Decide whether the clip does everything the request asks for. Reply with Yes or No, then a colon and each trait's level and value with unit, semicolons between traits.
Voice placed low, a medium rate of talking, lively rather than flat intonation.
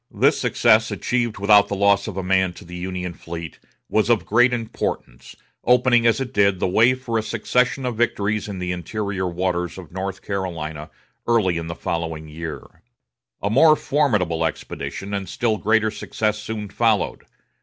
No: low, 100 Hz; average, 170 wpm; average, 4.1 semitones